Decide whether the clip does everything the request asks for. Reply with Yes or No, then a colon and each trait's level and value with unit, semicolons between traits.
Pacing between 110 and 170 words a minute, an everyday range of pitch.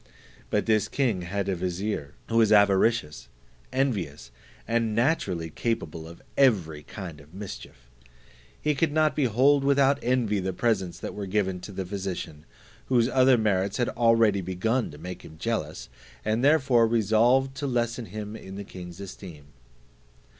Yes: average, 155 wpm; average, 4.8 semitones